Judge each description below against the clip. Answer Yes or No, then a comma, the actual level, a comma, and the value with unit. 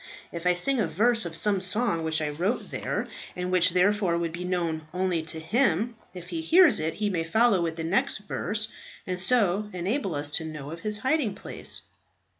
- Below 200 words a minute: No, fast, 205 wpm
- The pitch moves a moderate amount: Yes, average, 4.5 semitones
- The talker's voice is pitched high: No, medium, 180 Hz